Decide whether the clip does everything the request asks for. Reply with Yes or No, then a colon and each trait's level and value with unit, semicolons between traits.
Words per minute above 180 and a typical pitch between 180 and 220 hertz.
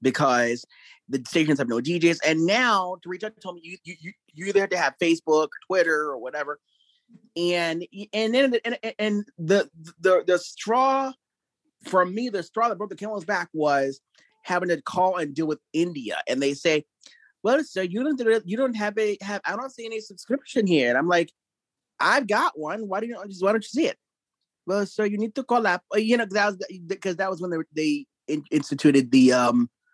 Yes: fast, 205 wpm; high, 190 Hz